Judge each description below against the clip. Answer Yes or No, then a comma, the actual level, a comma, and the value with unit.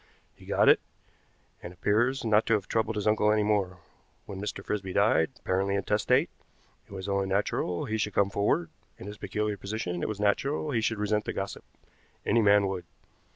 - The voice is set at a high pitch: No, low, 105 Hz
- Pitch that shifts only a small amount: Yes, narrow, 1.7 semitones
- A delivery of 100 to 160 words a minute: No, average, 190 wpm